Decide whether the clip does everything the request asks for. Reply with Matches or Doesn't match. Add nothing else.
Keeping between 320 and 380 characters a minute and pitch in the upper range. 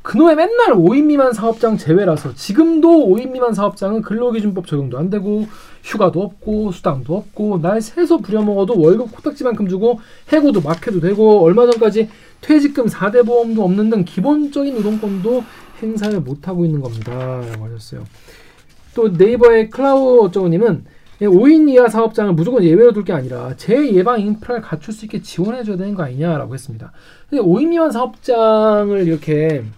Matches